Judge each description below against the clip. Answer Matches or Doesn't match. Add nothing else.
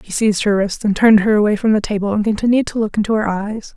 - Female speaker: Matches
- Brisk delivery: Matches